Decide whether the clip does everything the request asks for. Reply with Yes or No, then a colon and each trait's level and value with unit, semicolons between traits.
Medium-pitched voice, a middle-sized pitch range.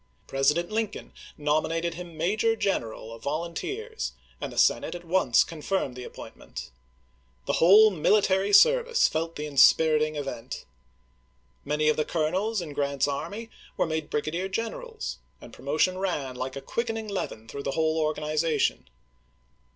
Yes: medium, 160 Hz; average, 4.9 semitones